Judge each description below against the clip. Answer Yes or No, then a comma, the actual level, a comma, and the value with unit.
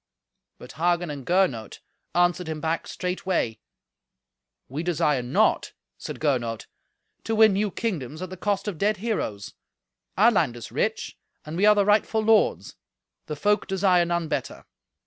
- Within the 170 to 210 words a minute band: No, average, 150 wpm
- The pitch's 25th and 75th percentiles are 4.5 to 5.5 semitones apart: Yes, average, 5.2 semitones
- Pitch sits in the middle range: Yes, medium, 175 Hz